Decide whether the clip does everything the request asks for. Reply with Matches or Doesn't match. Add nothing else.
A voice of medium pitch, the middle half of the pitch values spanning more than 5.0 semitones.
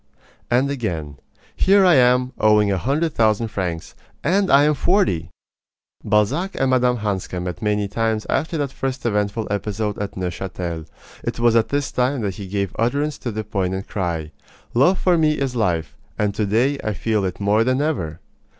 Doesn't match